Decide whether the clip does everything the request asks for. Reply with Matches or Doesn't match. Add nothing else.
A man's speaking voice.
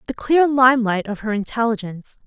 Doesn't match